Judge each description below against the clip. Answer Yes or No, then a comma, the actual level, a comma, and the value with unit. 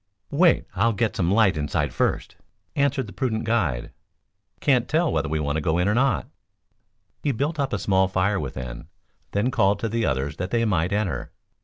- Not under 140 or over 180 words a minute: No, average, 195 wpm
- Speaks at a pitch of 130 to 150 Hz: No, low, 100 Hz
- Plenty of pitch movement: Yes, wide, 6.7 semitones